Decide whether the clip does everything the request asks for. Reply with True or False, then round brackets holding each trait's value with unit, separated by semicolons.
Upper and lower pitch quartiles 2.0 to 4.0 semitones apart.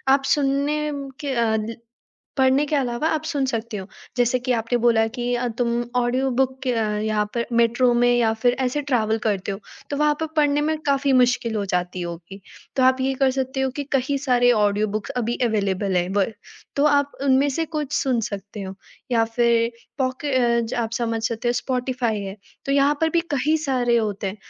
True (3.5 semitones)